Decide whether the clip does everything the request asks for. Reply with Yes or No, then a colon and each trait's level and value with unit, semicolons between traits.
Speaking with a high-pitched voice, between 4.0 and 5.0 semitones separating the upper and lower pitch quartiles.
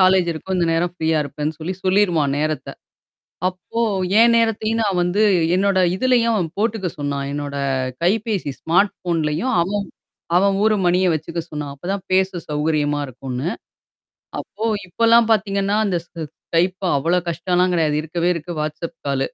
No: medium, 180 Hz; average, 4.3 semitones